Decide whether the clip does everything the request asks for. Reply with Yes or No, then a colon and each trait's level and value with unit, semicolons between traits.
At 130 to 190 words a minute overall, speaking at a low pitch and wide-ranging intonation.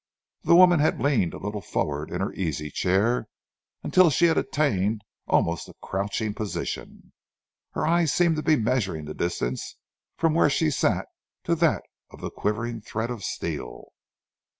Yes: average, 150 wpm; low, 115 Hz; wide, 8.3 semitones